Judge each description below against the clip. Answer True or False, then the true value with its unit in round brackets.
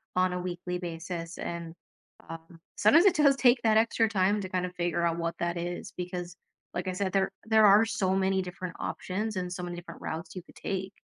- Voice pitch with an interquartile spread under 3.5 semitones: True (2.4 semitones)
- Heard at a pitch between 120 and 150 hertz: False (180 Hz)